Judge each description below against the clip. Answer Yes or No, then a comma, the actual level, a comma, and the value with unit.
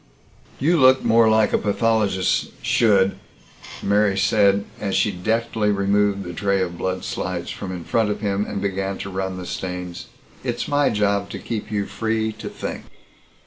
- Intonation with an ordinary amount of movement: No, narrow, 2.3 semitones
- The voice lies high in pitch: No, low, 100 Hz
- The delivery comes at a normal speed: Yes, average, 170 wpm